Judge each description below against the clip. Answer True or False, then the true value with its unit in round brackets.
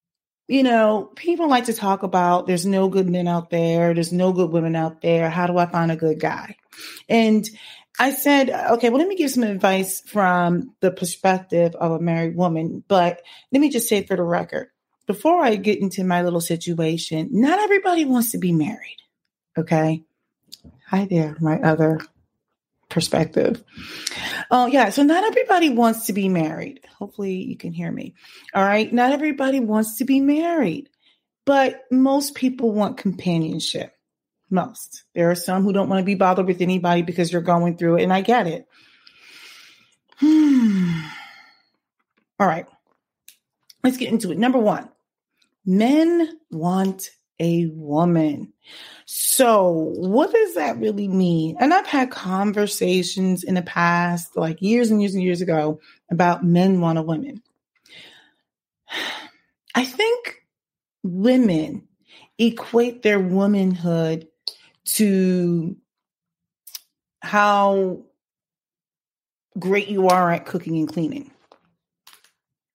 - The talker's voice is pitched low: False (190 Hz)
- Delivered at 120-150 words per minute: True (140 wpm)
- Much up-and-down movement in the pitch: True (5.9 semitones)